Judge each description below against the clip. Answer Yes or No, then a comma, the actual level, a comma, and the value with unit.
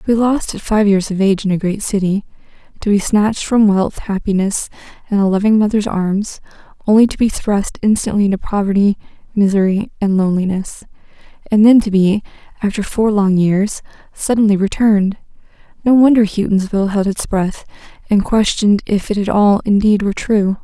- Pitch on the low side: No, high, 205 Hz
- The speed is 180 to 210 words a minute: No, average, 165 wpm